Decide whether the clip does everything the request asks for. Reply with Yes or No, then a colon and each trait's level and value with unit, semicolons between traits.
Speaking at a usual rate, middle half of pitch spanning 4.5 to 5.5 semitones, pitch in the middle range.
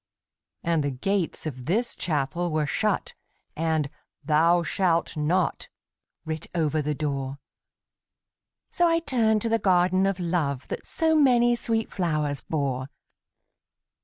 No: slow, 130 wpm; average, 5.2 semitones; medium, 170 Hz